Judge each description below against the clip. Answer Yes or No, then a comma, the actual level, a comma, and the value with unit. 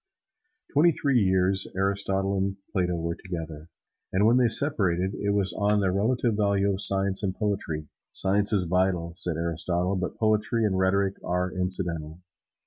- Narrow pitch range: Yes, narrow, 2.2 semitones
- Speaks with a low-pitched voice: Yes, very low, 95 Hz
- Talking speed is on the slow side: No, average, 155 wpm